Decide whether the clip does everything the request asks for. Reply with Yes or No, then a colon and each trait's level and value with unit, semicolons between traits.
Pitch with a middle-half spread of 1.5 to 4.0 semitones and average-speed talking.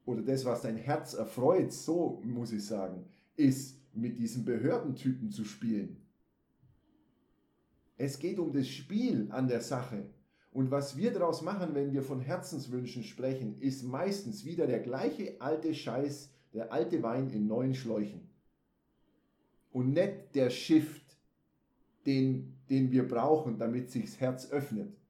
Yes: average, 3.5 semitones; average, 145 wpm